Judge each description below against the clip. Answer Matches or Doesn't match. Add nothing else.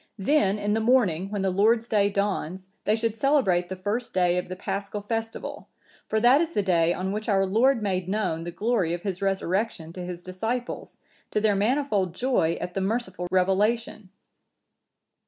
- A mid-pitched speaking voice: Doesn't match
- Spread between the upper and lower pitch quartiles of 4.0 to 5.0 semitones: Doesn't match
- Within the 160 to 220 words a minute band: Matches